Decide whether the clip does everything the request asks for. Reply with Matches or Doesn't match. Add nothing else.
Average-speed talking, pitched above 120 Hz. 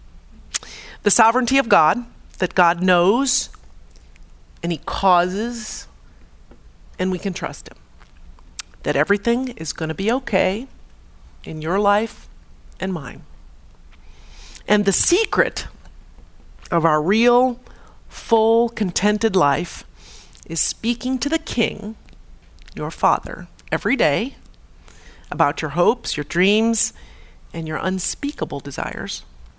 Doesn't match